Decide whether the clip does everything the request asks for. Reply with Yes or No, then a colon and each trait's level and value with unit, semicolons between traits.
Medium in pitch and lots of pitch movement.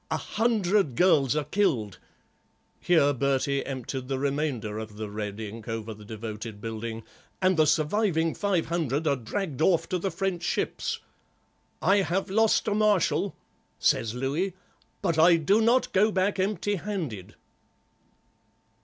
Yes: medium, 155 Hz; wide, 8.6 semitones